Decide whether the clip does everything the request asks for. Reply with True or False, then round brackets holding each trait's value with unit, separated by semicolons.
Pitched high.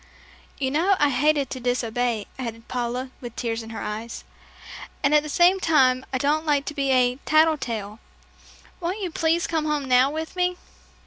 True (270 Hz)